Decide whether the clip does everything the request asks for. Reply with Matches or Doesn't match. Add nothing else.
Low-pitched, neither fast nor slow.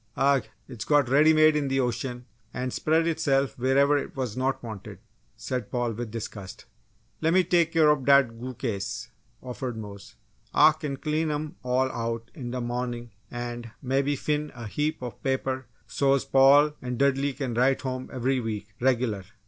Matches